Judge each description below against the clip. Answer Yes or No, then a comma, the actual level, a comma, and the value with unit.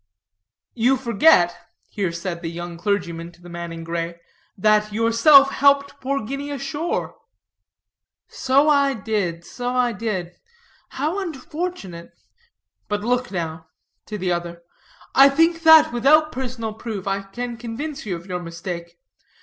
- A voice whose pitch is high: Yes, high, 220 Hz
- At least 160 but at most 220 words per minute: No, average, 140 wpm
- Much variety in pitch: Yes, wide, 7.9 semitones